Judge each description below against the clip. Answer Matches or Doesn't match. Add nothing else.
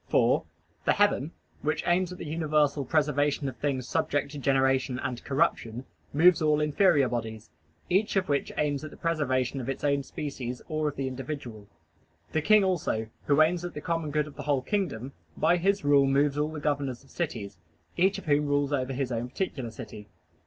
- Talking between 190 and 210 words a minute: Matches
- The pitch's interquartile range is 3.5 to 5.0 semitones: Doesn't match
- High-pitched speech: Doesn't match